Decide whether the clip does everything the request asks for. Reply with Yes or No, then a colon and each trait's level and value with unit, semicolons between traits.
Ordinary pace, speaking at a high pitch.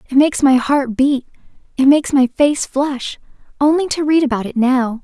Yes: average, 190 wpm; very high, 270 Hz